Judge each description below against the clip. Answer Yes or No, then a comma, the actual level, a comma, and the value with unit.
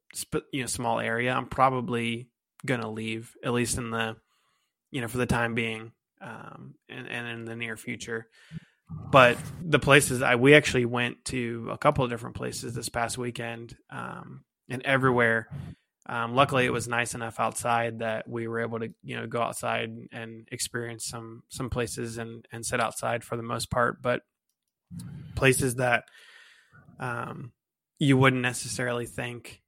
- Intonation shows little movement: Yes, narrow, 2.1 semitones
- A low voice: Yes, low, 120 Hz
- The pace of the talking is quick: No, average, 165 wpm